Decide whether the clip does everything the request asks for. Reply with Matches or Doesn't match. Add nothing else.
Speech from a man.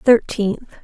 Doesn't match